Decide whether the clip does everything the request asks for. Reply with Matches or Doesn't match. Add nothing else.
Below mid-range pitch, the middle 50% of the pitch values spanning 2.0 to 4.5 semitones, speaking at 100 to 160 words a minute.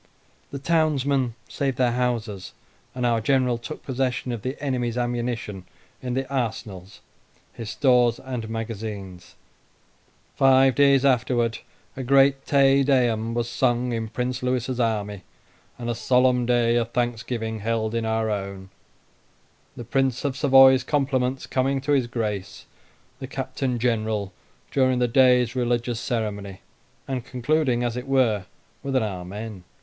Matches